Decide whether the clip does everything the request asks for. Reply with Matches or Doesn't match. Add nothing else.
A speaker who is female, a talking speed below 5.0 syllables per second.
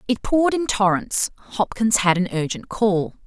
Matches